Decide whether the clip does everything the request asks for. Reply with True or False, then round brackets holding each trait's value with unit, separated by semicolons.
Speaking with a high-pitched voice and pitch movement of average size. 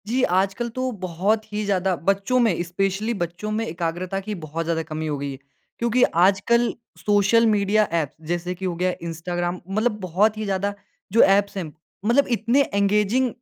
True (195 Hz; 3.6 semitones)